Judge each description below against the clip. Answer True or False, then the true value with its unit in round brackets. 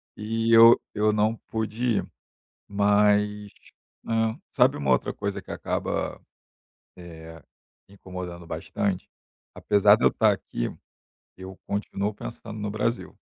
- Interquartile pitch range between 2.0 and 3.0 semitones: True (2.5 semitones)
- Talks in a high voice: False (105 Hz)